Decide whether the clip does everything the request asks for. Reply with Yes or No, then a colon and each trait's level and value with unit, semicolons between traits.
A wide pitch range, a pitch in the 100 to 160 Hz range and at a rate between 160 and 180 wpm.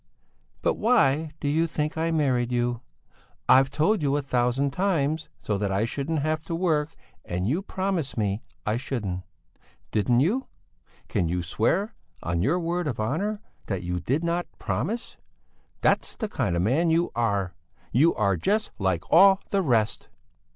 Yes: wide, 7.6 semitones; medium, 140 Hz; average, 165 wpm